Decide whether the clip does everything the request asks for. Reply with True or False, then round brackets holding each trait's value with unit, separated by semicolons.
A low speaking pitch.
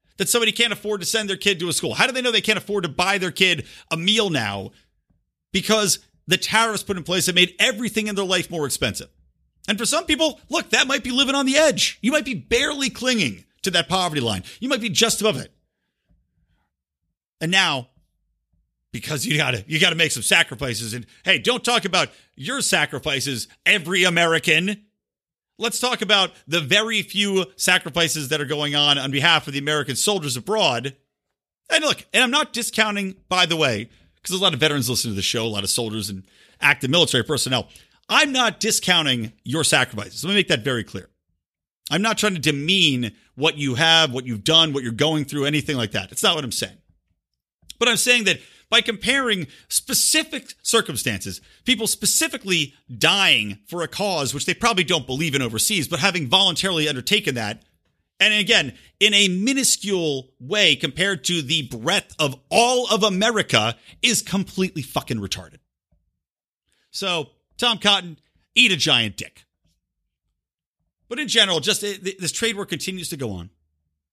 False (170 Hz)